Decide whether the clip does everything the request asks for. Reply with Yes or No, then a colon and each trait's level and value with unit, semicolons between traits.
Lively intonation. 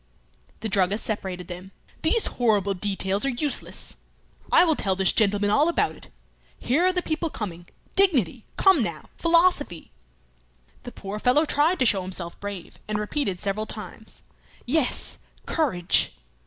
Yes: wide, 7.8 semitones